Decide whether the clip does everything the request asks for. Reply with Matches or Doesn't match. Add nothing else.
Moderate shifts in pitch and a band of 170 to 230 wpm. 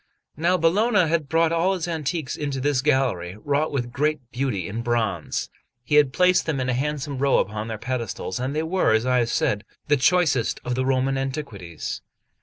Matches